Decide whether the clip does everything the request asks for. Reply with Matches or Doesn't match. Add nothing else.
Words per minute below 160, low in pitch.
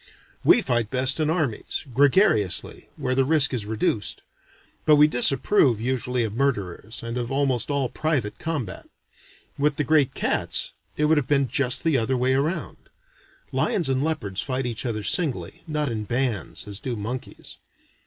Doesn't match